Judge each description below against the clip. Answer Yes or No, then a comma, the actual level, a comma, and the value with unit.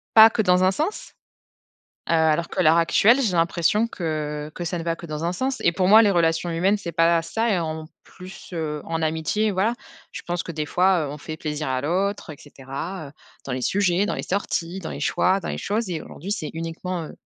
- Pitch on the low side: No, medium, 170 Hz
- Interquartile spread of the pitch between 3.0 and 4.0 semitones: Yes, average, 3.4 semitones